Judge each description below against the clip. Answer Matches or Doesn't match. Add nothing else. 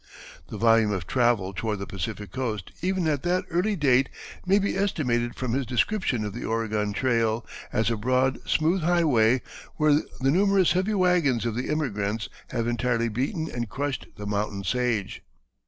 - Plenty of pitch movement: Matches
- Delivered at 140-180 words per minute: Matches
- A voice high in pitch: Doesn't match